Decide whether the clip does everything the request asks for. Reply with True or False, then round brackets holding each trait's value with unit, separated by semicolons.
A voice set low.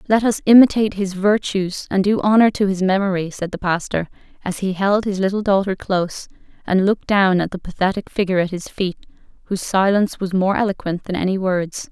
False (190 Hz)